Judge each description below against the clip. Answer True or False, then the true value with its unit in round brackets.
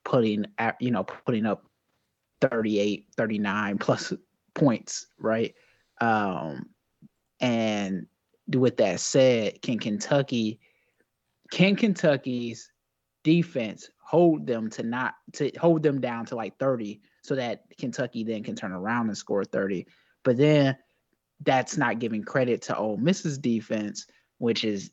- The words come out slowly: True (130 wpm)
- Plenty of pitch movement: False (4.1 semitones)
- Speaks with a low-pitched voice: True (115 Hz)